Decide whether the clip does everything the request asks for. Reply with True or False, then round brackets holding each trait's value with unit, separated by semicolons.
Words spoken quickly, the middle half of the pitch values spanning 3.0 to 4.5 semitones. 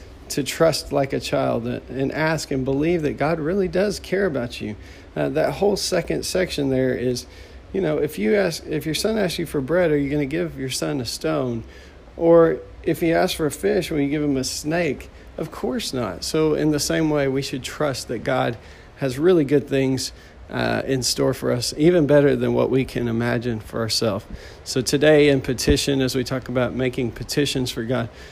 True (210 wpm; 4.0 semitones)